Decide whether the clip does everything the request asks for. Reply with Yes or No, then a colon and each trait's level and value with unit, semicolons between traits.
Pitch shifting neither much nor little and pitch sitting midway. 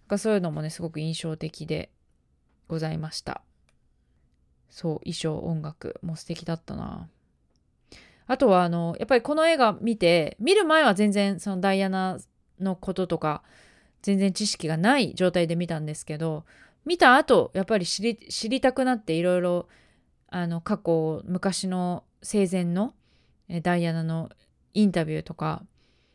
Yes: average, 4.1 semitones; medium, 175 Hz